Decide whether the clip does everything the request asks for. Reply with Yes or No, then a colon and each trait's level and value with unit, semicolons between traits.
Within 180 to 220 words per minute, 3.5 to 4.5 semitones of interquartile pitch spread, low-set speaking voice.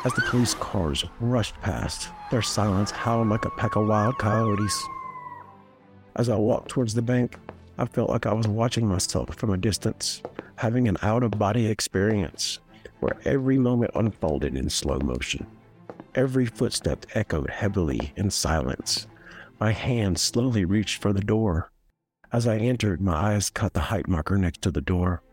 No: average, 165 wpm; average, 4.0 semitones; low, 105 Hz